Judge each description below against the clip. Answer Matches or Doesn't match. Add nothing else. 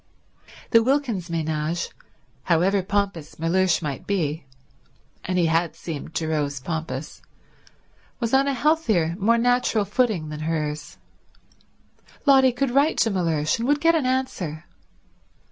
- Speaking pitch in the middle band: Matches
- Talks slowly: Matches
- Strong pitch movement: Matches